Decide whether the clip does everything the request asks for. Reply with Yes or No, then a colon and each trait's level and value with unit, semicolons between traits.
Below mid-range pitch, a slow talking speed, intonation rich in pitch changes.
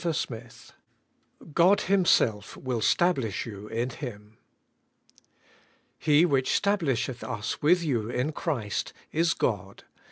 Yes: low, 130 Hz; slow, 120 wpm; wide, 7.0 semitones